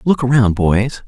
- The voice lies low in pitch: Yes, low, 115 Hz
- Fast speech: No, average, 170 wpm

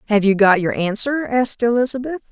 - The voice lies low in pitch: No, high, 230 Hz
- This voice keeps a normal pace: Yes, average, 180 wpm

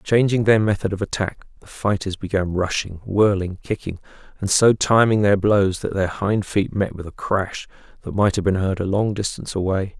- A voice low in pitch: Yes, low, 100 Hz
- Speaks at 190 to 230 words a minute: Yes, average, 200 wpm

